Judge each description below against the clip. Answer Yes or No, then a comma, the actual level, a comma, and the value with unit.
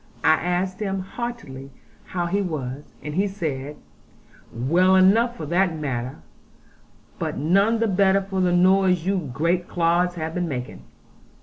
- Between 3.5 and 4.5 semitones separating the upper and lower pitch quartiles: Yes, average, 3.9 semitones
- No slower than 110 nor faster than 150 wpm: Yes, average, 145 wpm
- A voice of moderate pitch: Yes, medium, 180 Hz